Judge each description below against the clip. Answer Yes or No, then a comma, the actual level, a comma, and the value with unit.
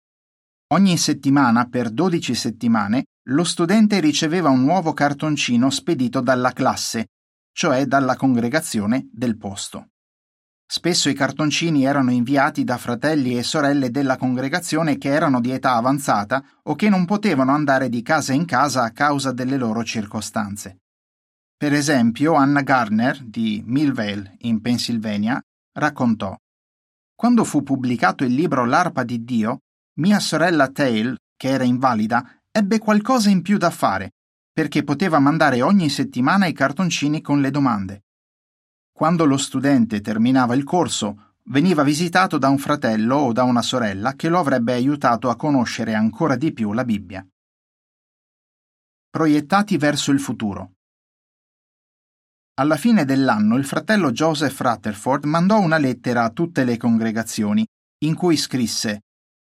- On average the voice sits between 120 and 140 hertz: Yes, low, 135 Hz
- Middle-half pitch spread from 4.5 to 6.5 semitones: Yes, average, 5.2 semitones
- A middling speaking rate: Yes, average, 135 wpm